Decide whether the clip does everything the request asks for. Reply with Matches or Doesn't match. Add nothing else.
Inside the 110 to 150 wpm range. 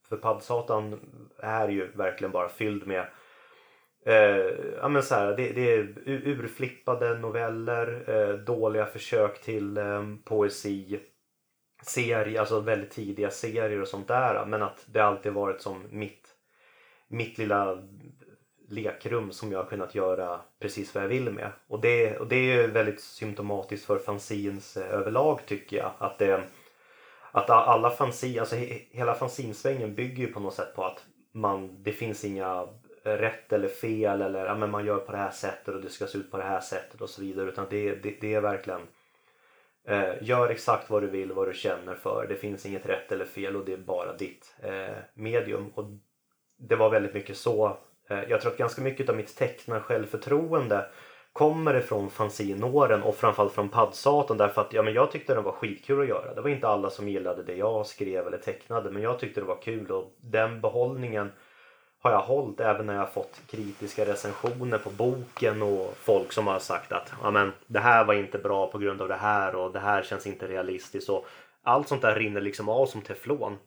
Doesn't match